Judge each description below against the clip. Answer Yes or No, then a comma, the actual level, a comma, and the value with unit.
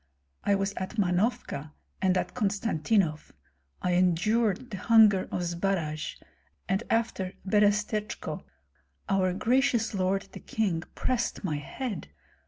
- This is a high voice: Yes, high, 195 Hz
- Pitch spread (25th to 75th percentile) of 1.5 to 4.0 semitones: Yes, average, 3.4 semitones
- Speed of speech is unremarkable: No, slow, 115 wpm